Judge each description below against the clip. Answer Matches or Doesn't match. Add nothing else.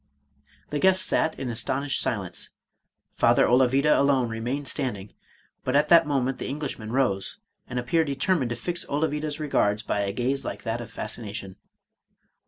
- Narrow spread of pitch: Doesn't match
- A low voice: Matches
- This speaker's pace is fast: Doesn't match